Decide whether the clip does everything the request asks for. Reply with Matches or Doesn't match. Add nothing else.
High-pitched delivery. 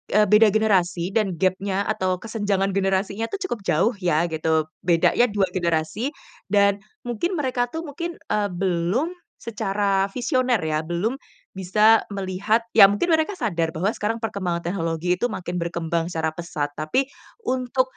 Matches